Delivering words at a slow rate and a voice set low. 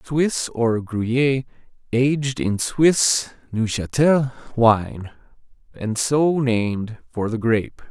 Yes: slow, 105 wpm; low, 125 Hz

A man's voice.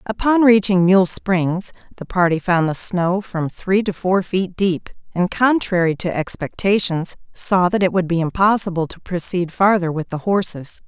No: female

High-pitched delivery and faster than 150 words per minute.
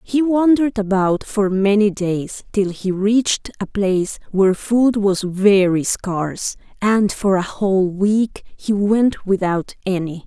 No: high, 200 Hz; average, 145 wpm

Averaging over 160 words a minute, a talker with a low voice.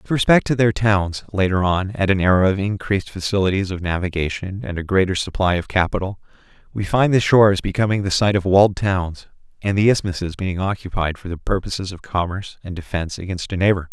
Yes: average, 200 wpm; very low, 95 Hz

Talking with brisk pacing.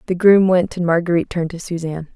Yes: fast, 225 wpm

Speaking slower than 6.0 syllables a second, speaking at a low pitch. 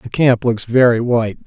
Yes: 5.2 syllables/s; low, 120 Hz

